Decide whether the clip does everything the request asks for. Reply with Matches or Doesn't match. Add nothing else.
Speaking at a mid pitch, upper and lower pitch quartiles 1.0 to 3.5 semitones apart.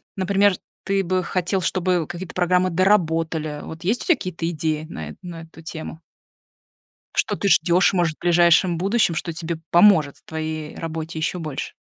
Matches